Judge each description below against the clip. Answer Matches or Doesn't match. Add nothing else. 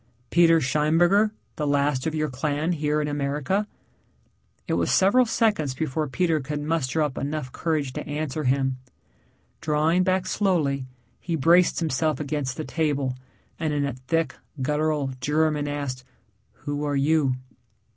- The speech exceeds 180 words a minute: Doesn't match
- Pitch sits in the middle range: Matches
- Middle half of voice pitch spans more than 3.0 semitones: Doesn't match